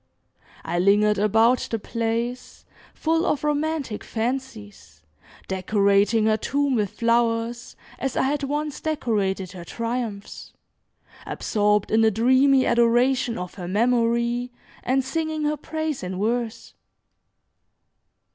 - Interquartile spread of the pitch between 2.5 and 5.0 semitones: Yes, average, 4.1 semitones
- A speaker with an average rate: No, slow, 115 wpm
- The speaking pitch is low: No, high, 235 Hz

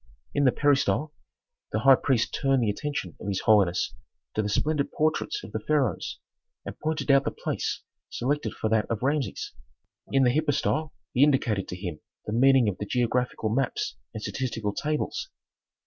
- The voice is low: Yes, low, 130 Hz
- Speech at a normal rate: Yes, average, 170 wpm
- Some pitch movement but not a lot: Yes, average, 5.0 semitones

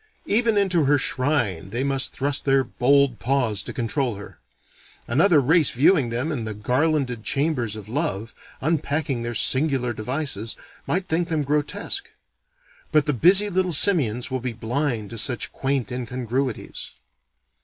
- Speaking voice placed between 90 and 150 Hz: Yes, low, 135 Hz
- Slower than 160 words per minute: Yes, average, 145 wpm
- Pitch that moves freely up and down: No, average, 4.4 semitones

